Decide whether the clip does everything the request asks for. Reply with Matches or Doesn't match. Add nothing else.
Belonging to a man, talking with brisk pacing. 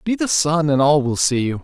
Matches